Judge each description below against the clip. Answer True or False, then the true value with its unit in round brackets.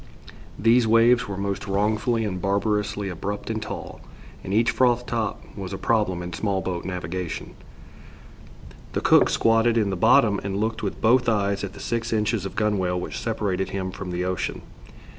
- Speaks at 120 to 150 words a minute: False (175 wpm)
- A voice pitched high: False (105 Hz)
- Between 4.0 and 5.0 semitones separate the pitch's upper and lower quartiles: False (2.9 semitones)